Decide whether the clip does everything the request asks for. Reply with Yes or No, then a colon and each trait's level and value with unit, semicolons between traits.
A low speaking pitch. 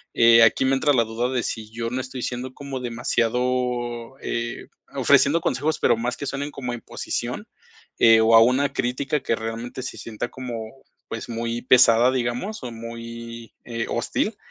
Yes: low, 120 Hz